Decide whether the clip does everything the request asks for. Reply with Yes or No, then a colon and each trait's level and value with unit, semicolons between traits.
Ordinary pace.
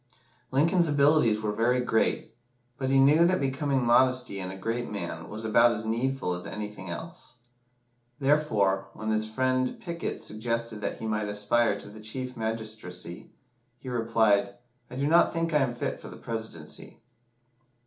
Yes: average, 160 wpm